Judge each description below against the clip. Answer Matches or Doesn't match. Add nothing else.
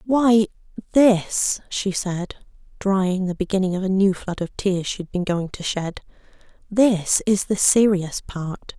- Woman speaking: Matches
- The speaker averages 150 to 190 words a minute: Matches